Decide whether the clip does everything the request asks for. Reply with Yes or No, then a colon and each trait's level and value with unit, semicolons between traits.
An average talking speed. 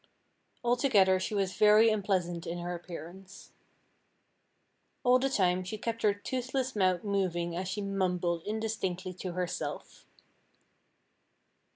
No: slow, 115 wpm